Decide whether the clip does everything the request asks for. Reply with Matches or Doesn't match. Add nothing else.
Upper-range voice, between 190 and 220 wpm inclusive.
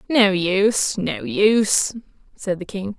Doesn't match